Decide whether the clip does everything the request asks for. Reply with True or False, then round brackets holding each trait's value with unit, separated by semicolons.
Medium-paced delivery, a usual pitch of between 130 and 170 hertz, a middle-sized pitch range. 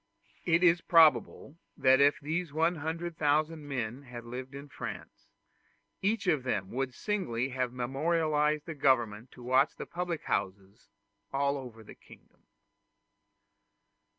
False (125 wpm; 140 Hz; 4.5 semitones)